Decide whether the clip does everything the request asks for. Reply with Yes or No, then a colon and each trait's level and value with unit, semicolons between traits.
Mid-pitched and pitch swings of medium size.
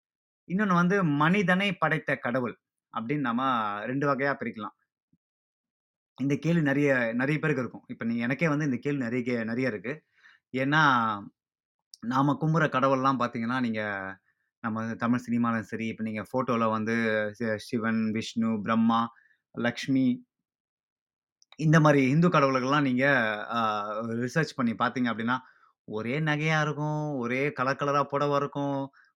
No: low, 130 Hz; average, 4.1 semitones